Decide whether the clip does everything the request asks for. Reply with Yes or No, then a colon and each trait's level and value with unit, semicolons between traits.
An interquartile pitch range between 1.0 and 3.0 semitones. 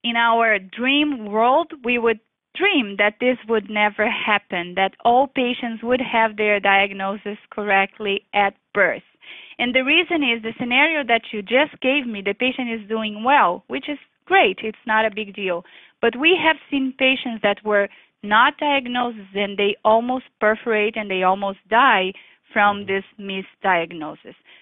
No: average, 4.1 semitones